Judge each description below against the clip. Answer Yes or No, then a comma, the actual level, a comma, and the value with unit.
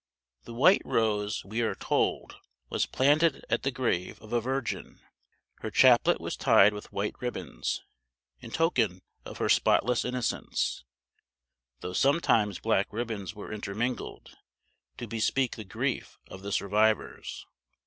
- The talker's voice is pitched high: No, low, 115 Hz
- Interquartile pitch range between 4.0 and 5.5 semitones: No, average, 3.3 semitones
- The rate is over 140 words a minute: No, slow, 135 wpm